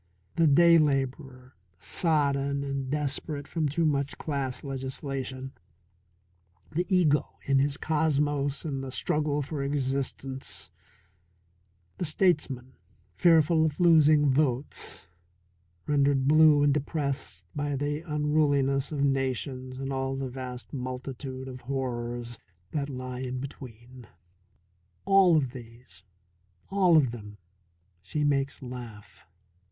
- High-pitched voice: No, medium, 140 Hz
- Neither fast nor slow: No, slow, 115 wpm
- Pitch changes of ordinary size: No, narrow, 2.3 semitones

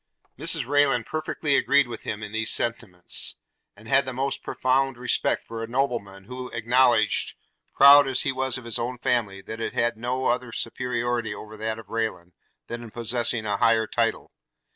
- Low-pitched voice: Yes, low, 120 Hz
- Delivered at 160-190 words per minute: Yes, average, 180 wpm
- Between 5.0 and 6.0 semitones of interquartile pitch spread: No, narrow, 2.6 semitones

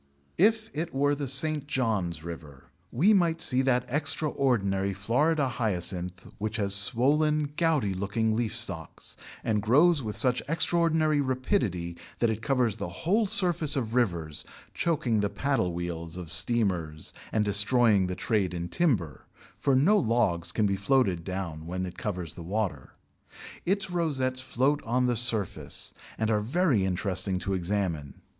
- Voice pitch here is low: Yes, low, 110 Hz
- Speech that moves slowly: No, average, 150 wpm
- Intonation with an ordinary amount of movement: No, wide, 7.2 semitones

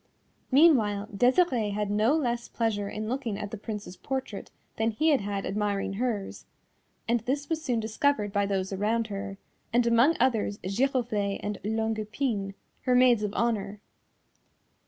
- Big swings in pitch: No, average, 3.5 semitones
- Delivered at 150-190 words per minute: Yes, average, 155 wpm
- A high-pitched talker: Yes, high, 220 Hz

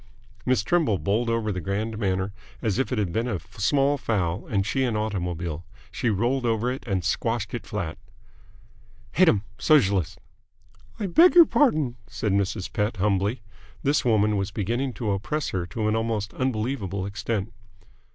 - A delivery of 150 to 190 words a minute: Yes, average, 165 wpm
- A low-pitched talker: Yes, low, 110 Hz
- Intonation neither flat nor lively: Yes, average, 3.7 semitones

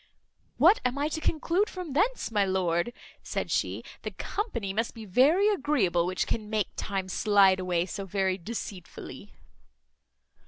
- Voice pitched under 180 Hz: No, high, 210 Hz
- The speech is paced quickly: No, average, 150 wpm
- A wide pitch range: Yes, wide, 7.8 semitones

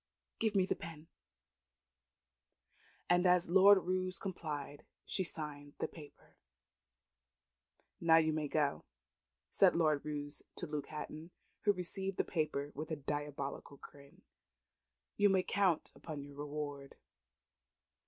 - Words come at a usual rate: No, slow, 125 wpm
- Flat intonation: No, average, 3.8 semitones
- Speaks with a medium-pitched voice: Yes, medium, 155 Hz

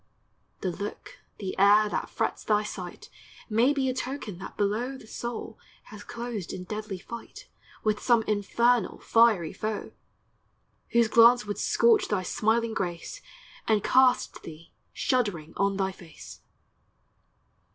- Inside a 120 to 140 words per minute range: Yes, slow, 135 wpm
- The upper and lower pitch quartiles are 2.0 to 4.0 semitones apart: Yes, average, 3.1 semitones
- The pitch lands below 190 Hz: No, high, 215 Hz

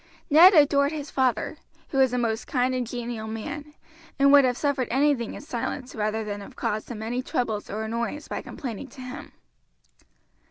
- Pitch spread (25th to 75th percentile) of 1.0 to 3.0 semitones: No, average, 4.0 semitones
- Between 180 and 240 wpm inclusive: Yes, average, 185 wpm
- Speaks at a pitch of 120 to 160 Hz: No, very high, 250 Hz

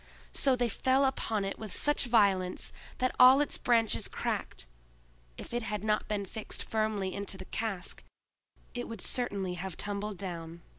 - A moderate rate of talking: Yes, average, 160 wpm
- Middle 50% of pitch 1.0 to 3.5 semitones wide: No, average, 3.9 semitones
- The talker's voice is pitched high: Yes, high, 210 Hz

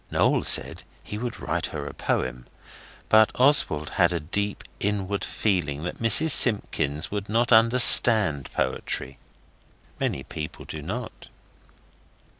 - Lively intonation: Yes, wide, 6.9 semitones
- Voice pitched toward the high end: No, low, 100 Hz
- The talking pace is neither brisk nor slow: No, slow, 125 wpm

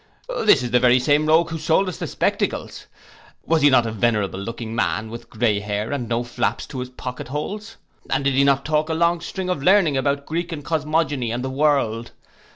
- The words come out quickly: Yes, fast, 215 wpm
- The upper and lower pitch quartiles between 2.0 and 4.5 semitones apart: No, average, 5.0 semitones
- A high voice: No, medium, 140 Hz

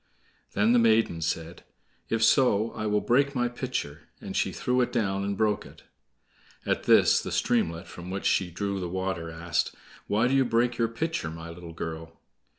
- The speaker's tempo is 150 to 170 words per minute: No, average, 185 wpm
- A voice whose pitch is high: No, low, 100 Hz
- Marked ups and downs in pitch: Yes, wide, 5.8 semitones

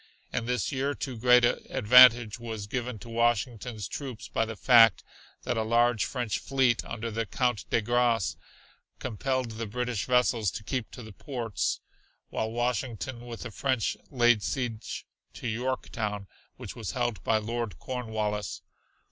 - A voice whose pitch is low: Yes, low, 120 Hz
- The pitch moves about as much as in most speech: No, narrow, 2.2 semitones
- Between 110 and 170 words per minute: Yes, average, 155 wpm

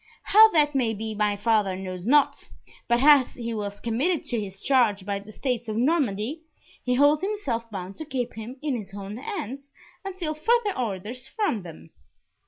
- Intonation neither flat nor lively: No, wide, 6.1 semitones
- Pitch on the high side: Yes, high, 240 Hz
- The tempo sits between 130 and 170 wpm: No, average, 180 wpm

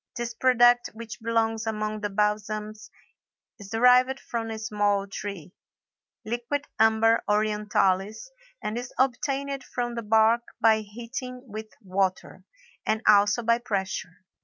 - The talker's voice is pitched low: No, high, 220 Hz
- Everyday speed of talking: No, slow, 120 wpm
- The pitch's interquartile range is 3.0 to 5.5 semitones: No, narrow, 2.4 semitones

